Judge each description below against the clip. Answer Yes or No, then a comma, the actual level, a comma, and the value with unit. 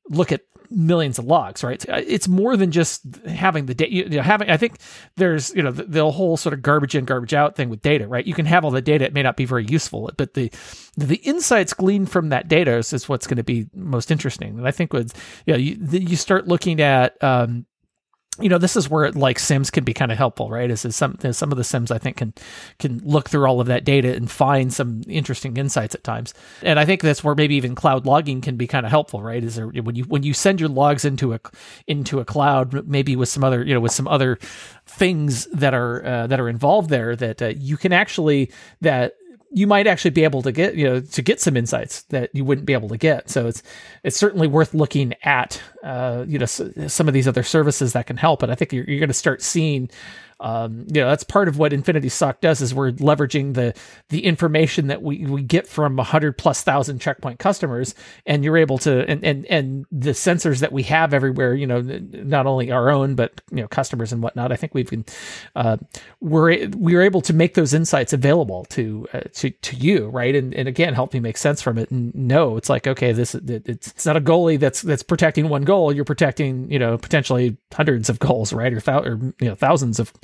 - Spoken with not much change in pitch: No, average, 4.2 semitones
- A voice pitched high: No, medium, 140 Hz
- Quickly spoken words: Yes, fast, 245 wpm